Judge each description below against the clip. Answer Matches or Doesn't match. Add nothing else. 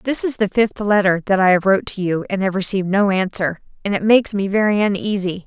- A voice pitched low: Doesn't match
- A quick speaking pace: Matches